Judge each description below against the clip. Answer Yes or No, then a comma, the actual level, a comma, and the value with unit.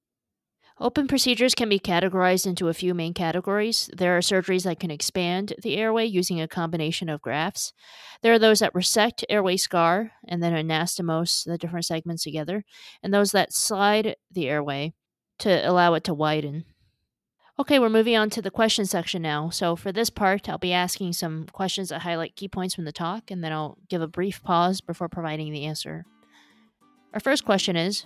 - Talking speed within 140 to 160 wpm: No, average, 190 wpm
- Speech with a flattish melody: No, average, 3.5 semitones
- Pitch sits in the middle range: Yes, medium, 180 Hz